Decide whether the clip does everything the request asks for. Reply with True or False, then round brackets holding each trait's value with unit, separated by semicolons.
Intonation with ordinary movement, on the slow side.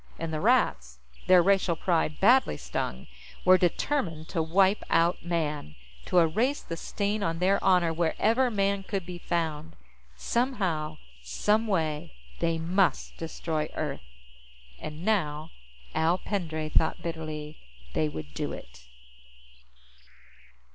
True (4.0 semitones; 125 wpm)